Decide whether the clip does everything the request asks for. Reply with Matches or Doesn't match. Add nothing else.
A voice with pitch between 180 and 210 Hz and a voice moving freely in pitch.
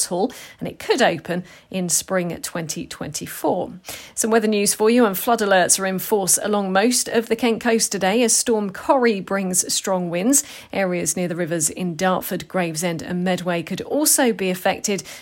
Doesn't match